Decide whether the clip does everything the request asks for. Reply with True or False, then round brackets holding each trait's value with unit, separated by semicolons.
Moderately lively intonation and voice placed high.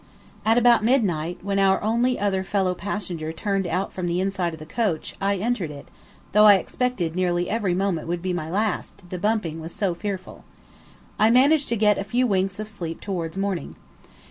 True (3.3 semitones; 195 Hz)